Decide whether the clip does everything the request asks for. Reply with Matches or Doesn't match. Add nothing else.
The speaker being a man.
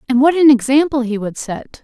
Doesn't match